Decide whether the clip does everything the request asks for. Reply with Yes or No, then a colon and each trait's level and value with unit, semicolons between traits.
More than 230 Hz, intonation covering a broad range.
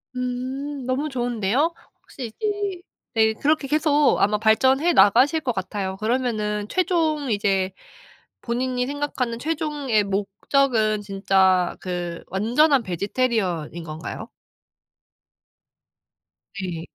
Yes: high, 240 Hz; wide, 6.1 semitones